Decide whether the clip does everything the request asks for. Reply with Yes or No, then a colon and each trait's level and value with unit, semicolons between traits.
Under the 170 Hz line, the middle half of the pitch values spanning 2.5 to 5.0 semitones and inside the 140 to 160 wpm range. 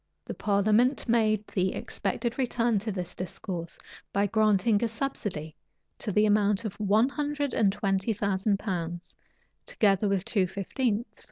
No: high, 205 Hz; average, 2.9 semitones; average, 145 wpm